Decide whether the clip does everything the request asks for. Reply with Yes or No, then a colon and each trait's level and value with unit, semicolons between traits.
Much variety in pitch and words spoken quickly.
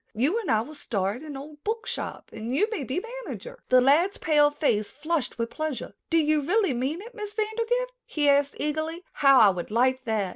Yes: wide, 6.3 semitones; fast, 210 wpm